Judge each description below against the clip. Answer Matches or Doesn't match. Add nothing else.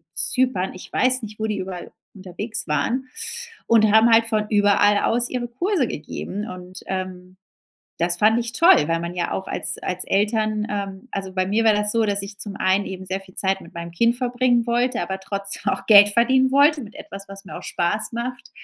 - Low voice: Doesn't match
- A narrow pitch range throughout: Doesn't match